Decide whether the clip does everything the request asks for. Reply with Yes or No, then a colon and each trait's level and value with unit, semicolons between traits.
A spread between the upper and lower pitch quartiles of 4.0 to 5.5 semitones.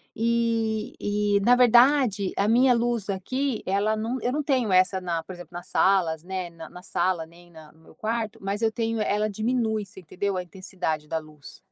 Yes: average, 4.3 semitones